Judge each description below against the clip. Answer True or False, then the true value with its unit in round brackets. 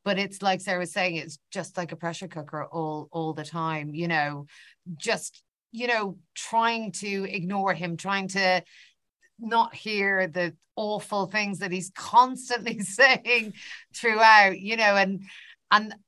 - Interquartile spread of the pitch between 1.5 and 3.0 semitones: False (3.7 semitones)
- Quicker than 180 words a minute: False (155 wpm)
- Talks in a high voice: True (195 Hz)